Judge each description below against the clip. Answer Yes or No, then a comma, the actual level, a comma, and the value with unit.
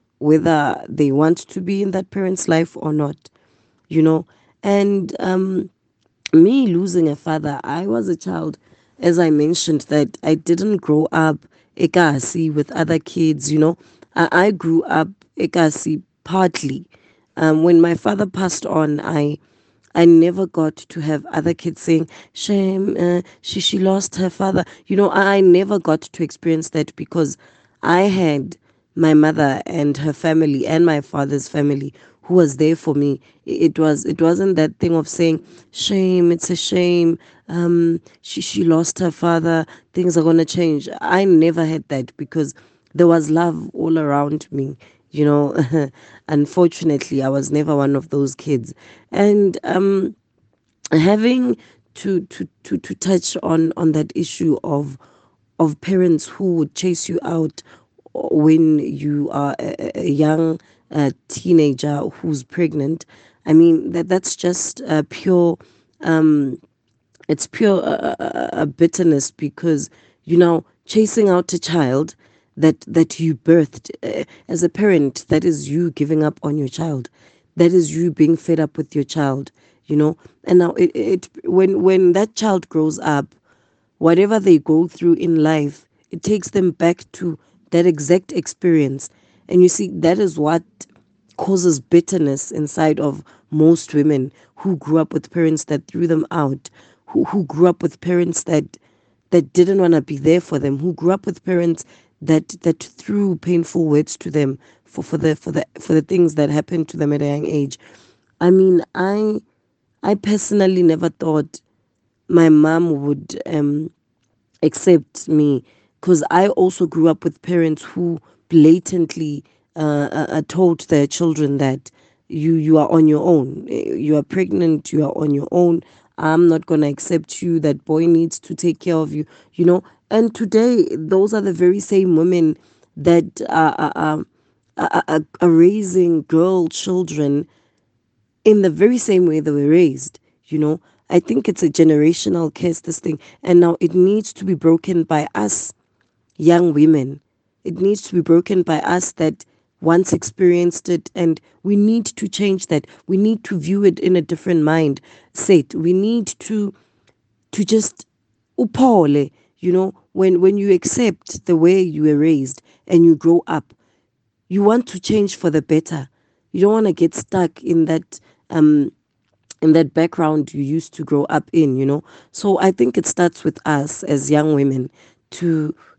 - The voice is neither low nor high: Yes, medium, 165 Hz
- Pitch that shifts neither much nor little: Yes, average, 3.0 semitones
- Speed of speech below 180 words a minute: Yes, average, 165 wpm